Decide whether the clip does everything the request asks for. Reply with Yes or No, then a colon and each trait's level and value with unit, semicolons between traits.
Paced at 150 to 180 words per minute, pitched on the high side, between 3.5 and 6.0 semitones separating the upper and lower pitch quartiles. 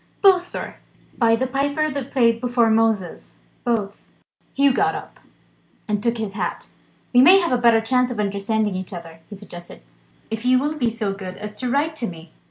No: average, 190 wpm; high, 230 Hz; average, 4.3 semitones